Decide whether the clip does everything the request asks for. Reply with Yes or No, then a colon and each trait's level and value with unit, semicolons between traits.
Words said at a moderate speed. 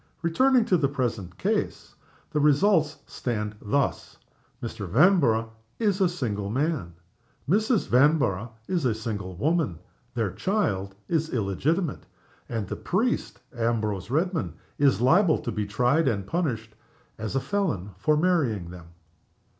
No: slow, 130 wpm